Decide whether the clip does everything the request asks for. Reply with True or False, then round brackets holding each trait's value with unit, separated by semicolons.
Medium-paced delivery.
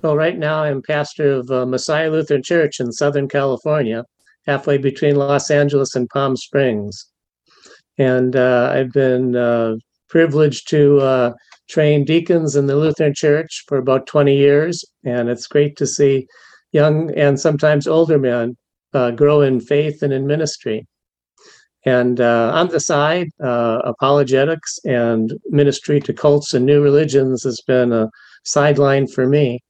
True (150 wpm)